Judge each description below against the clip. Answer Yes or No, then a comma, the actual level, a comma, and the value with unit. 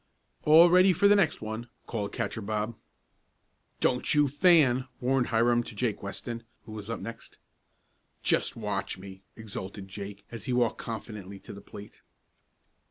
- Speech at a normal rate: Yes, average, 155 wpm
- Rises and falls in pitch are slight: No, average, 3.9 semitones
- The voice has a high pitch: No, low, 115 Hz